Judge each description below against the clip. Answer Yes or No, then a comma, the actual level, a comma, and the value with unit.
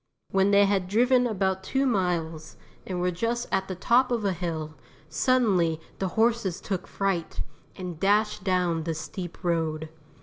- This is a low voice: No, high, 190 Hz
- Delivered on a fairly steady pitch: No, average, 3.8 semitones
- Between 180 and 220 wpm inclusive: No, average, 160 wpm